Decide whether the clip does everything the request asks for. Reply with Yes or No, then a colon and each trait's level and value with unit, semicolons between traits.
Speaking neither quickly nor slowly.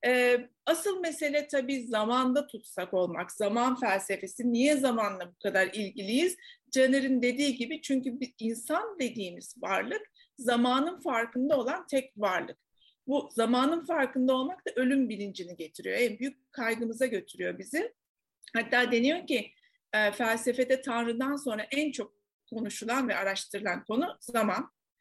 Yes: average, 125 wpm